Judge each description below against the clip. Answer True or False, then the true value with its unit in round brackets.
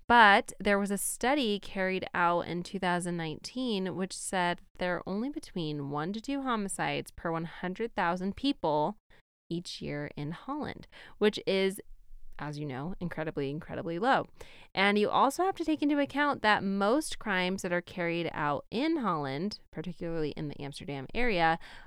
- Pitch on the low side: False (185 Hz)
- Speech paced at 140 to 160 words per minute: True (155 wpm)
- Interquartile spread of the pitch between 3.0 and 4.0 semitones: False (4.8 semitones)